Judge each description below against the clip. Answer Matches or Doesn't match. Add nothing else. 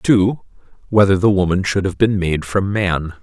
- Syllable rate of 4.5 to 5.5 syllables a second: Matches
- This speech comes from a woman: Doesn't match